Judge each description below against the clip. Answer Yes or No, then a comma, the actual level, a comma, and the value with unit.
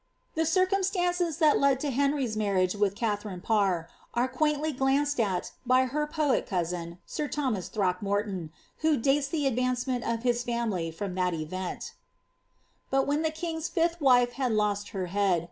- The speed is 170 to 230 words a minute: No, average, 160 wpm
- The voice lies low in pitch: No, high, 245 Hz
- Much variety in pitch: Yes, wide, 6.7 semitones